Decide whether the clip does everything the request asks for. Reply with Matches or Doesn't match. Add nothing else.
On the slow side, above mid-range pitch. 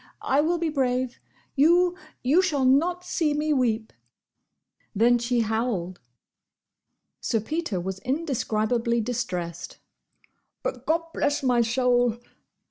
Matches